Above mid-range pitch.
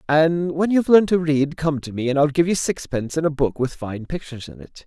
No: medium, 155 Hz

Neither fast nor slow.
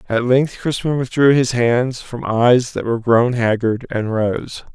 Yes: average, 175 wpm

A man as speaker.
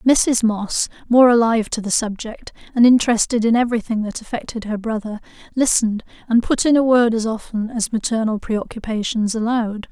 No: female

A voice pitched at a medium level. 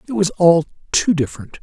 Yes: medium, 170 Hz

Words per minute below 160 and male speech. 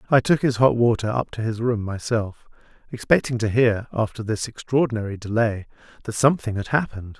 No: average, 175 wpm; male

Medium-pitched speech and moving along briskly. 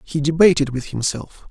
No: medium, 150 Hz; average, 160 wpm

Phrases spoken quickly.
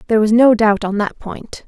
Yes: fast, 250 wpm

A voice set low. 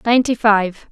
No: high, 215 Hz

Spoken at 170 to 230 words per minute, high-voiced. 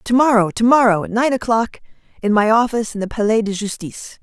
Yes: average, 200 wpm; high, 220 Hz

